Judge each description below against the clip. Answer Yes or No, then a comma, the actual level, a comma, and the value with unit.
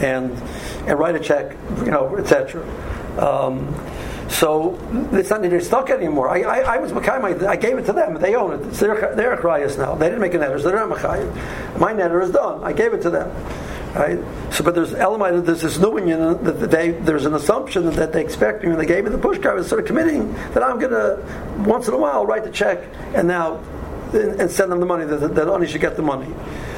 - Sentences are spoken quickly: Yes, fast, 225 wpm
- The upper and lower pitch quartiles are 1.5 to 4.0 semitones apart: Yes, average, 3.4 semitones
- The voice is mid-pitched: Yes, medium, 175 Hz